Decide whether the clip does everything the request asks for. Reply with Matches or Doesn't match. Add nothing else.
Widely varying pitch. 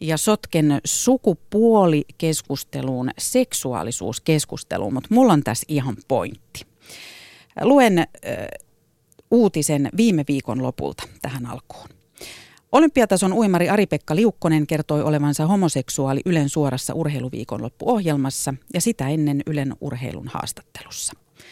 Matches